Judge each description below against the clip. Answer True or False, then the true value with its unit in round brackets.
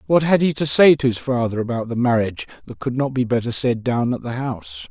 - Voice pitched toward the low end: True (120 Hz)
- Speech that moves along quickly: True (255 wpm)